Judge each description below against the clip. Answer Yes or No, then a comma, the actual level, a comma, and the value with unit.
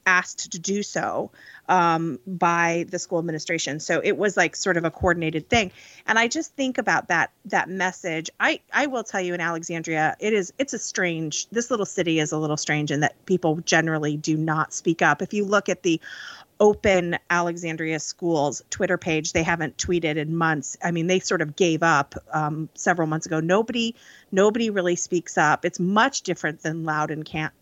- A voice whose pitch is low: No, medium, 170 Hz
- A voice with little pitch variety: No, average, 3.2 semitones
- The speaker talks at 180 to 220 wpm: Yes, average, 200 wpm